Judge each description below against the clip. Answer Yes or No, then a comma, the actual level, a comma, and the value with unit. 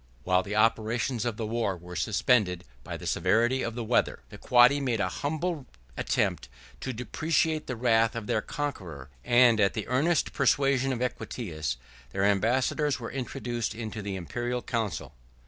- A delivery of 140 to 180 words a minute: Yes, average, 160 wpm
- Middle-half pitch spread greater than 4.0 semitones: No, average, 3.6 semitones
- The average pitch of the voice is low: Yes, low, 120 Hz